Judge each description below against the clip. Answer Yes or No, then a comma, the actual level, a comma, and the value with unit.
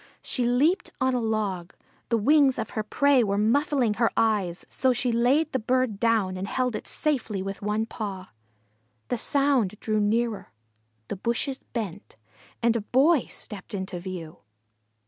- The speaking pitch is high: Yes, high, 225 Hz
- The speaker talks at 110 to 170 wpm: Yes, average, 160 wpm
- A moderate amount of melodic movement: Yes, average, 4.1 semitones